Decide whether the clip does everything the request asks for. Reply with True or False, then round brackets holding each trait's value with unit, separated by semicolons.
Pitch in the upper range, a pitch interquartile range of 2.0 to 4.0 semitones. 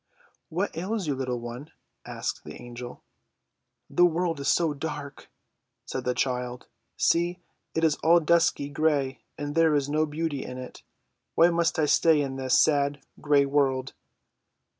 False (145 Hz; 3.6 semitones)